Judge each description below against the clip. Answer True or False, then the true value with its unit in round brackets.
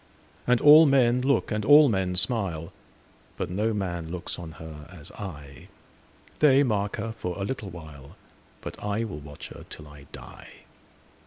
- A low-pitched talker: True (95 Hz)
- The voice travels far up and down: True (6.5 semitones)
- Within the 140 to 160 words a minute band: True (150 wpm)